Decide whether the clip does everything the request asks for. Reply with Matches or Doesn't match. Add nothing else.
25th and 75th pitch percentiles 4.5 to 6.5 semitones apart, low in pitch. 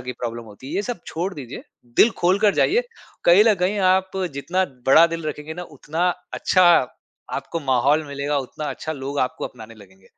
Doesn't match